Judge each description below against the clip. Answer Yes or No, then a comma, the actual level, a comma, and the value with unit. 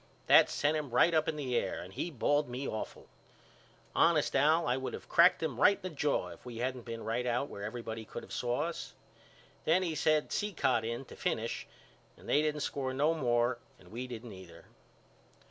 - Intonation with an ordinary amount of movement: Yes, average, 4.5 semitones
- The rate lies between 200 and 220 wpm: Yes, fast, 205 wpm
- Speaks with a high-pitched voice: No, low, 130 Hz